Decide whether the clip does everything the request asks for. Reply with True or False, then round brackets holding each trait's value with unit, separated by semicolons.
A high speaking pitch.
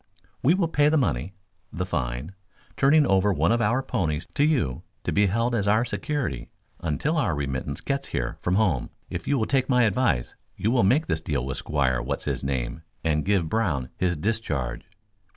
False (95 Hz)